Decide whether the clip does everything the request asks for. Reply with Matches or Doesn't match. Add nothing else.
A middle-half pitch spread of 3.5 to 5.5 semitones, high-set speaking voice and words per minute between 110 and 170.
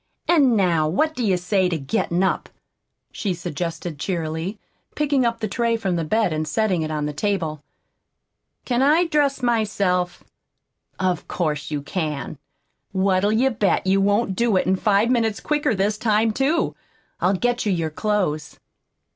Matches